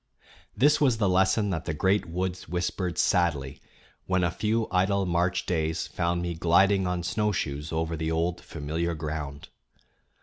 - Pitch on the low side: Yes, very low, 85 Hz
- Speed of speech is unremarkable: Yes, average, 155 wpm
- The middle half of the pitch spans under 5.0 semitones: Yes, average, 2.7 semitones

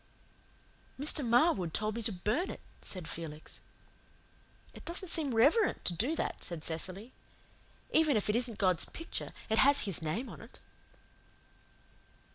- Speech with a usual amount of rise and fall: No, wide, 7.8 semitones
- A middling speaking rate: Yes, average, 145 wpm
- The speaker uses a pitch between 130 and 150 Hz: No, high, 225 Hz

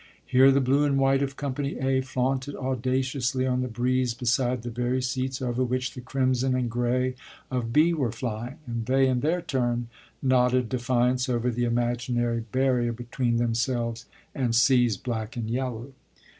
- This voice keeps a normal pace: Yes, average, 165 wpm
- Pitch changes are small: Yes, narrow, 1.6 semitones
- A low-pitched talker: Yes, low, 125 Hz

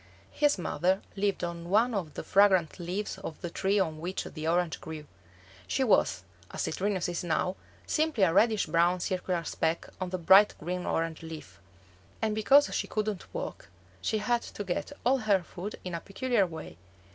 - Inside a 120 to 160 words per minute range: No, average, 180 wpm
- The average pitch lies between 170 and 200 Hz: Yes, medium, 185 Hz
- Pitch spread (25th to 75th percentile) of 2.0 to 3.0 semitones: No, average, 3.7 semitones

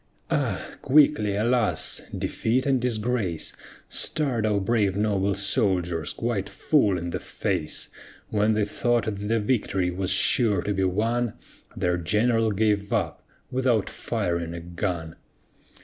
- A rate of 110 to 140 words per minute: Yes, slow, 135 wpm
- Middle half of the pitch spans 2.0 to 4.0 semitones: Yes, average, 3.7 semitones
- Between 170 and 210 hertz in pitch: No, low, 105 Hz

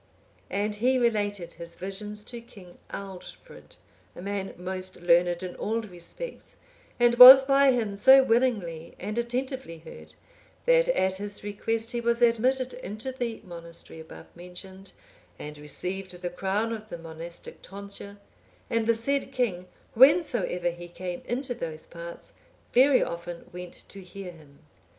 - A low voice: No, high, 200 Hz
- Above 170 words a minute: No, average, 145 wpm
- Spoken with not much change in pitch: No, average, 5.2 semitones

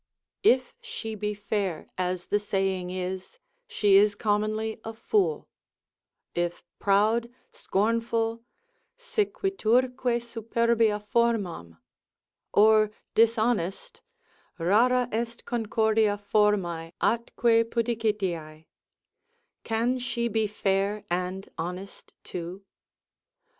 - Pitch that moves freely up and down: No, average, 3.2 semitones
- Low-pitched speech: No, high, 215 Hz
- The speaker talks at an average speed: No, slow, 85 wpm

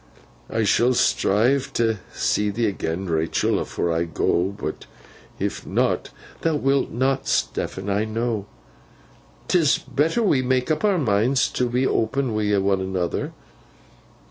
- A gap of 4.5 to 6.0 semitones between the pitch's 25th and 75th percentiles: Yes, average, 5.2 semitones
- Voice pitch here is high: No, low, 115 Hz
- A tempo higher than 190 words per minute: No, average, 145 wpm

